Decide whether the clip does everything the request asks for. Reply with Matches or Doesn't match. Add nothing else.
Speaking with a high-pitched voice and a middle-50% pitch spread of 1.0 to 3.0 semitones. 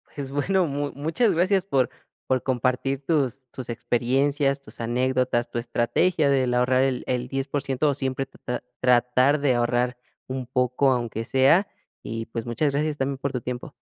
Doesn't match